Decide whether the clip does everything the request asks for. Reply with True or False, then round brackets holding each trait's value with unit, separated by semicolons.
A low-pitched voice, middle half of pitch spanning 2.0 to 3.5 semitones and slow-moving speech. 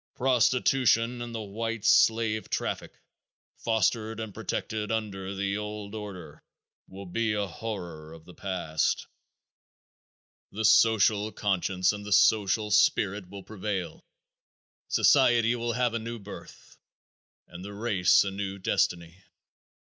True (105 Hz; 2.7 semitones; 125 wpm)